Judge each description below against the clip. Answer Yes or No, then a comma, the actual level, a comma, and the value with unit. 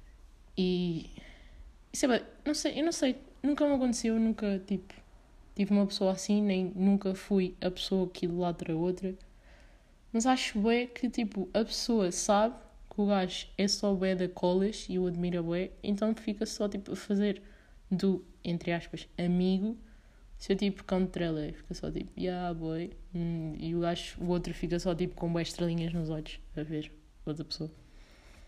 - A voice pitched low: No, medium, 185 Hz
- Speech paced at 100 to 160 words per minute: No, average, 175 wpm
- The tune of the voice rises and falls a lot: No, average, 3.3 semitones